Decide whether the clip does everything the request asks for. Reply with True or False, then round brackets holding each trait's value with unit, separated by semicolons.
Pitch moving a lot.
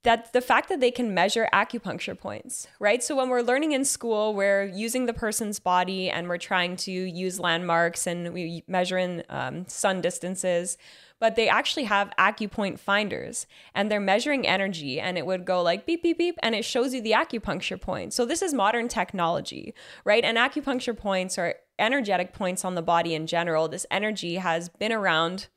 False (4.5 semitones)